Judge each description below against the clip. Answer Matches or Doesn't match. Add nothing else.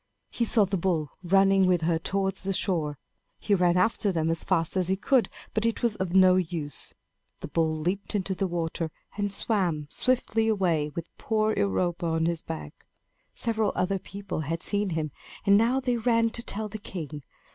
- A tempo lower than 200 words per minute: Matches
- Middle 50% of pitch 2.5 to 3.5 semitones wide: Doesn't match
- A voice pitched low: Doesn't match